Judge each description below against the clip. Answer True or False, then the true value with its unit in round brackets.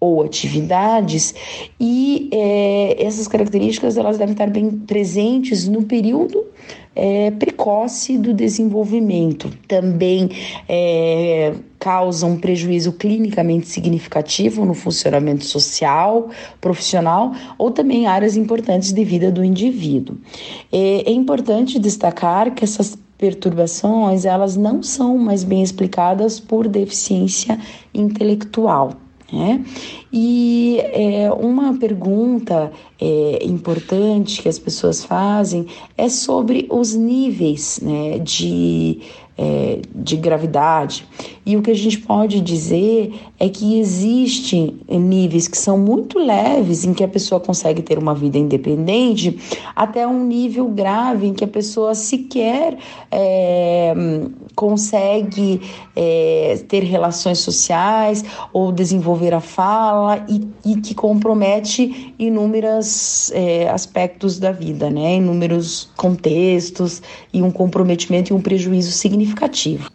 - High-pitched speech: True (200 Hz)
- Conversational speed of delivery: False (115 wpm)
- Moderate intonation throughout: True (4.0 semitones)